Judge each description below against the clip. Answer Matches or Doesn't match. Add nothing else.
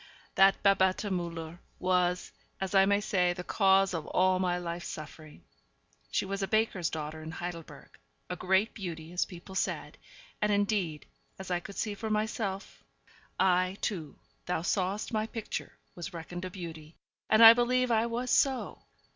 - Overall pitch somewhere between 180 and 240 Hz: Matches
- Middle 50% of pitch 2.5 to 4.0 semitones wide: Matches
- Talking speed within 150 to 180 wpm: Matches